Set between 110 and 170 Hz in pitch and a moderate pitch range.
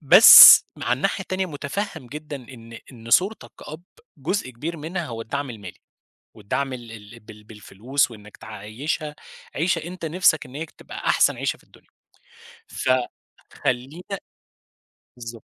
No: low, 135 Hz; wide, 5.7 semitones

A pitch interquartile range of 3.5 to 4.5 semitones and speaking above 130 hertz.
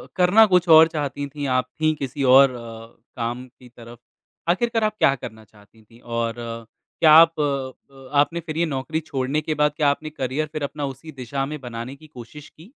Yes: average, 4.2 semitones; medium, 140 Hz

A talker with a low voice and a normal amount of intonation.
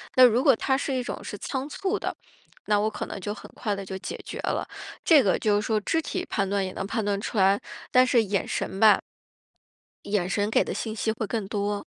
No: high, 215 Hz; average, 3.9 semitones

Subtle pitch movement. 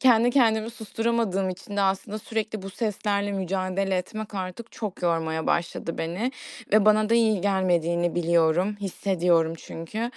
No: average, 3.7 semitones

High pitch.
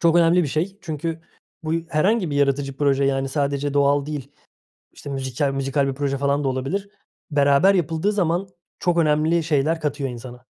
No: medium, 145 Hz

